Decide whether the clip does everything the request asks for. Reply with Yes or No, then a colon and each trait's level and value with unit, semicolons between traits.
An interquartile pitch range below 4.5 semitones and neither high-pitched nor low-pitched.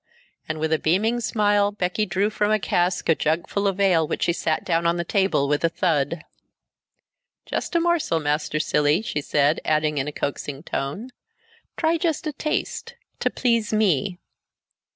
No: wide, 5.5 semitones; medium, 175 Hz